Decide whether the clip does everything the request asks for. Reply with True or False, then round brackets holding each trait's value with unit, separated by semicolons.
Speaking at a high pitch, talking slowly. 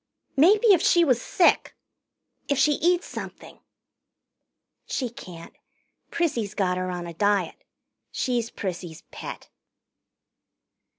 True (230 Hz; 115 wpm)